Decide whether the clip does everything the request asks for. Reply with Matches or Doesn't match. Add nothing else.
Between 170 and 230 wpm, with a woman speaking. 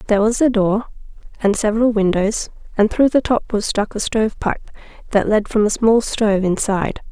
Matches